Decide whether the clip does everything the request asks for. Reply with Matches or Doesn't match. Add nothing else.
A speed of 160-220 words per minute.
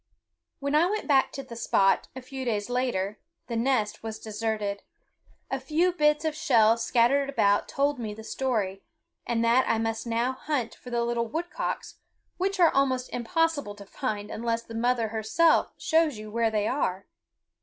Matches